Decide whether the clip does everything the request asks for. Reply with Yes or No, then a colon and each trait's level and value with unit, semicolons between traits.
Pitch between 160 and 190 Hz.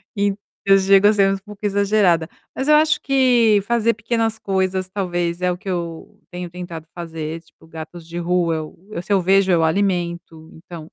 Yes: medium, 185 Hz